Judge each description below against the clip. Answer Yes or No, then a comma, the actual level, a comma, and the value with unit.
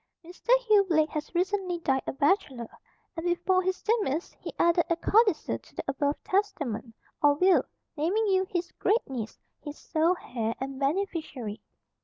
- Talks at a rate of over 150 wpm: Yes, average, 160 wpm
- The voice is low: No, very high, 335 Hz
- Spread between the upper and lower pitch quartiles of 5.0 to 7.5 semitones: Yes, average, 5.3 semitones